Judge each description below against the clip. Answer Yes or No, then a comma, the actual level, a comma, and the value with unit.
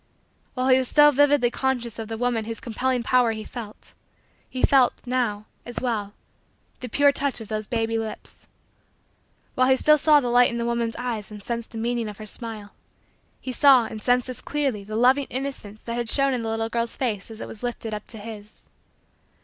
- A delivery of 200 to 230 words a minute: Yes, fast, 205 wpm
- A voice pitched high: Yes, high, 235 Hz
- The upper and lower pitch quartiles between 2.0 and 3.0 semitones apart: Yes, narrow, 2.5 semitones